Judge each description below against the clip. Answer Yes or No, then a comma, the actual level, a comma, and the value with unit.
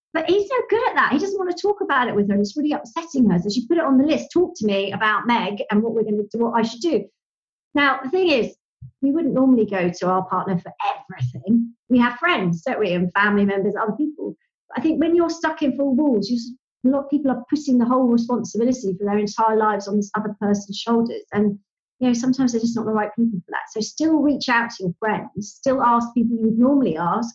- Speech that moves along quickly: Yes, fast, 260 wpm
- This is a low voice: No, high, 235 Hz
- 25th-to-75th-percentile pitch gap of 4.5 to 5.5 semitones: Yes, average, 5.0 semitones